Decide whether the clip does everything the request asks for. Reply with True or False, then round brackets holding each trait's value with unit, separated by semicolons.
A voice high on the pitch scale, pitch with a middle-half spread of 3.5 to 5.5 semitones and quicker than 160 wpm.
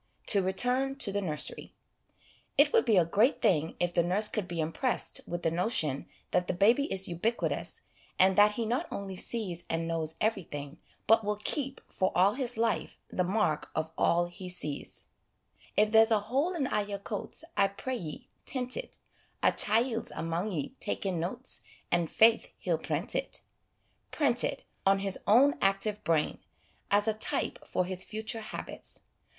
True (200 Hz; 4.7 semitones; 180 wpm)